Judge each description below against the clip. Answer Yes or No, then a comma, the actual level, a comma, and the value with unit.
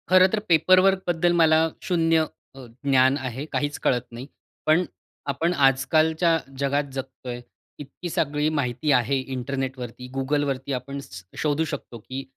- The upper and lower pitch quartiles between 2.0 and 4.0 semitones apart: Yes, average, 3.5 semitones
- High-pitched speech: No, medium, 140 Hz